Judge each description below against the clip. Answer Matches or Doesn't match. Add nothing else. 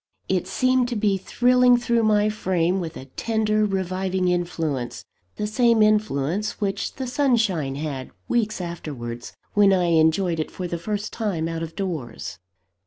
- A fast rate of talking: Doesn't match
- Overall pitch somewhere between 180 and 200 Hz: Matches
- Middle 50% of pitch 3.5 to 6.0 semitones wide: Matches